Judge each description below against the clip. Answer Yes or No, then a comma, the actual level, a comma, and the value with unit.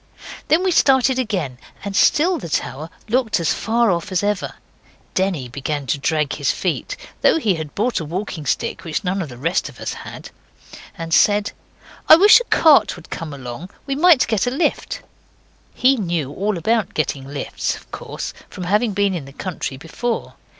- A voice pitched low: No, high, 190 Hz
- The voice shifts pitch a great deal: Yes, wide, 7.5 semitones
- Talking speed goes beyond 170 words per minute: Yes, average, 185 wpm